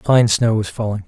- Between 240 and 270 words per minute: No, fast, 225 wpm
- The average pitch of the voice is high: No, low, 110 Hz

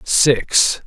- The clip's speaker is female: No, male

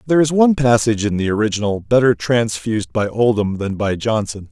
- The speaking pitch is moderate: No, low, 115 Hz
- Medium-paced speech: Yes, average, 185 wpm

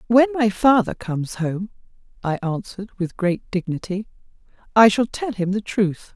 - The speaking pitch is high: Yes, high, 205 Hz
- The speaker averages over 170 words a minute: No, average, 155 wpm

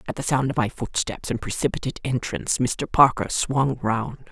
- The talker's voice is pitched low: Yes, low, 125 Hz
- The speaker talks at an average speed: Yes, average, 180 wpm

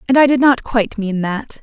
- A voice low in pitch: No, high, 235 Hz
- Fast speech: Yes, fast, 260 wpm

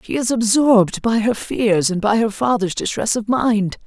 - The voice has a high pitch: Yes, high, 220 Hz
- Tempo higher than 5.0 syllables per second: No, 4.6 syllables/s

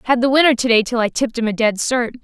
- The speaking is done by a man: No, female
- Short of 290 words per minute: No, fast, 295 wpm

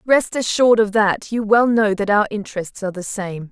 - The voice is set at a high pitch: Yes, high, 210 Hz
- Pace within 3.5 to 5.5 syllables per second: Yes, 5.3 syllables/s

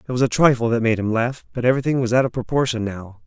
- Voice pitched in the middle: No, low, 120 Hz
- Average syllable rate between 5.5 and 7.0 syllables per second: Yes, 6.7 syllables/s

